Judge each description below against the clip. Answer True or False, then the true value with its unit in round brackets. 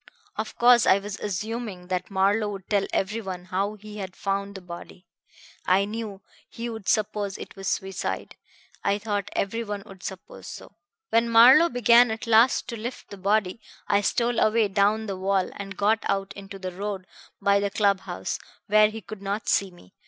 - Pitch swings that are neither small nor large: False (2.2 semitones)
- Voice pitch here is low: False (200 Hz)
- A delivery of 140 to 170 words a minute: False (180 wpm)